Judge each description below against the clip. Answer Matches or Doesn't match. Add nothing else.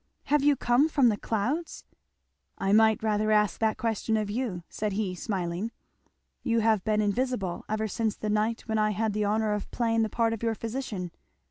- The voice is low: Doesn't match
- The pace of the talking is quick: Doesn't match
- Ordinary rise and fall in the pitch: Doesn't match